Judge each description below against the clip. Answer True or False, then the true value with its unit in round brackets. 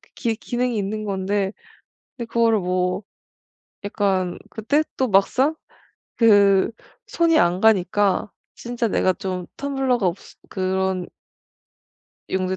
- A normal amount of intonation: True (3.8 semitones)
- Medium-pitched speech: False (205 Hz)